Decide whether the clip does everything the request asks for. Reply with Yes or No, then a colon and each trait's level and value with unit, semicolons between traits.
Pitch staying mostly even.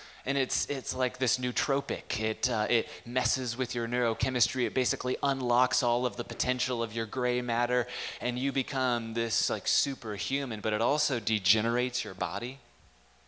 Yes: narrow, 2.0 semitones